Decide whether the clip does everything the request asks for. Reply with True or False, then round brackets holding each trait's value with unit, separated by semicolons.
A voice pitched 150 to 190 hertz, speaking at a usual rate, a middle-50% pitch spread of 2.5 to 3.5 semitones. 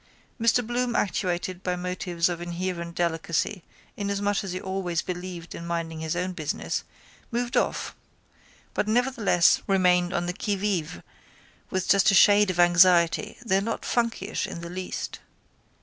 True (185 Hz; 150 wpm; 2.8 semitones)